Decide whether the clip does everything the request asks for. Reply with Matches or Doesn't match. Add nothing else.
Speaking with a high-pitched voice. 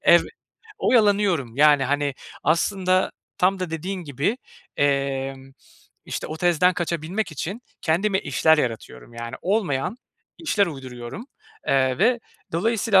Doesn't match